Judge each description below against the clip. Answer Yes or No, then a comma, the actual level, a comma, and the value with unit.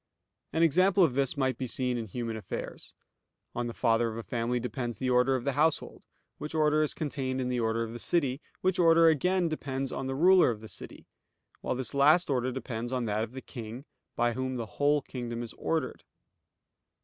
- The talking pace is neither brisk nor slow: No, fast, 210 wpm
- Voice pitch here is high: No, low, 130 Hz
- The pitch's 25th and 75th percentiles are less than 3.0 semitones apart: No, average, 4.0 semitones